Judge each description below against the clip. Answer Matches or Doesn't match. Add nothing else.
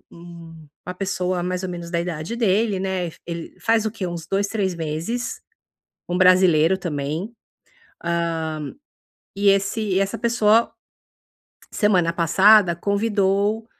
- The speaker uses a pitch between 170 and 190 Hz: Matches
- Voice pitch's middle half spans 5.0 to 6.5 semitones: Doesn't match